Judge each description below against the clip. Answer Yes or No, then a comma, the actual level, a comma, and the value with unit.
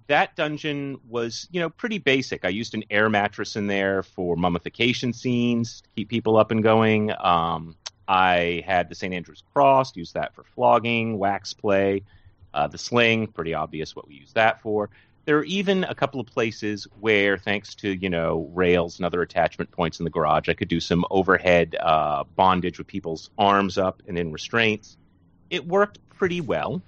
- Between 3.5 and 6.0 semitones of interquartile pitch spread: Yes, average, 4.9 semitones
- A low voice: Yes, low, 100 Hz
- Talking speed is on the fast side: No, average, 190 wpm